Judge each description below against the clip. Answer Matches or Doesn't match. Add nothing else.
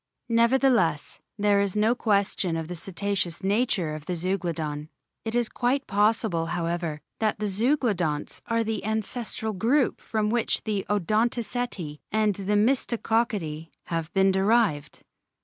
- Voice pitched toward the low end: Doesn't match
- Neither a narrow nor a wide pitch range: Matches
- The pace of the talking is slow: Matches